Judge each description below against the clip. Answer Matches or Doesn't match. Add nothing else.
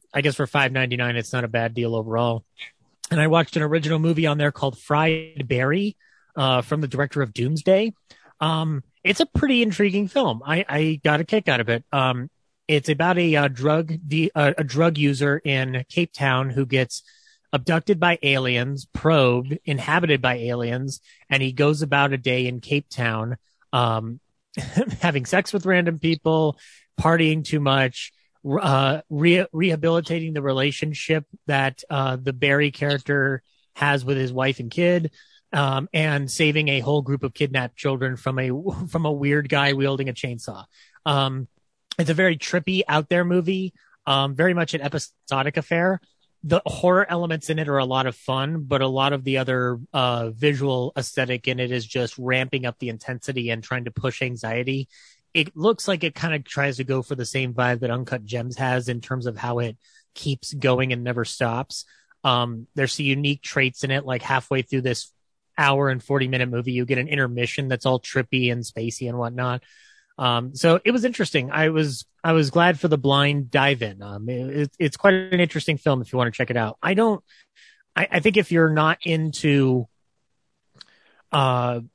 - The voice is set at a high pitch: Doesn't match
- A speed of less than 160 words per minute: Doesn't match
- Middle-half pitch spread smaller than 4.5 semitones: Matches